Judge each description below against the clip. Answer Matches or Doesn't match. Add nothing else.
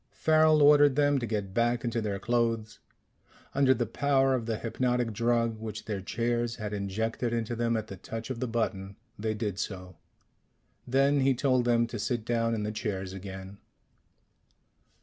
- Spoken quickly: Doesn't match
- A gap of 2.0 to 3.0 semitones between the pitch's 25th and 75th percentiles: Matches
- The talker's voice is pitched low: Matches